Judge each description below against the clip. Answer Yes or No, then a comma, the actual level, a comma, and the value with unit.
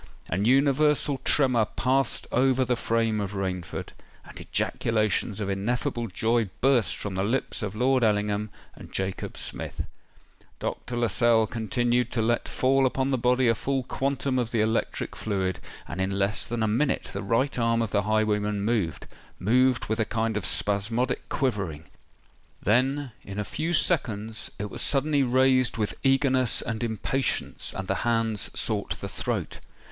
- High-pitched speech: No, low, 115 Hz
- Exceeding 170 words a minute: No, average, 155 wpm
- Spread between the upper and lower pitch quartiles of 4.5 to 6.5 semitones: No, average, 3.7 semitones